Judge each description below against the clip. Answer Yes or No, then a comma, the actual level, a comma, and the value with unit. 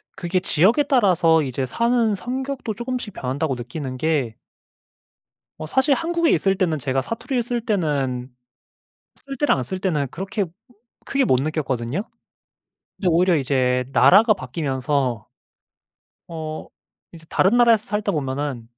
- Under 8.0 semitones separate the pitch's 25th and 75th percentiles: No, wide, 9.0 semitones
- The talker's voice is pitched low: No, medium, 170 Hz